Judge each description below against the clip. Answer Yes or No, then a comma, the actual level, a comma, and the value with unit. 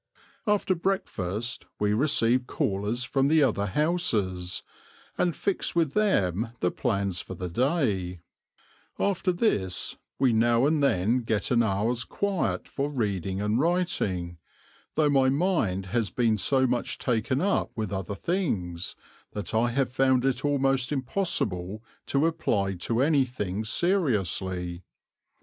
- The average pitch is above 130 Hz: No, low, 120 Hz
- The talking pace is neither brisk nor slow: No, slow, 130 wpm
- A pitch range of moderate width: No, wide, 6.7 semitones